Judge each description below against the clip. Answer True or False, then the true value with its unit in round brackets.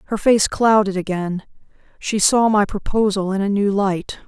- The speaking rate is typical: True (155 wpm)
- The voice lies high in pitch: True (200 Hz)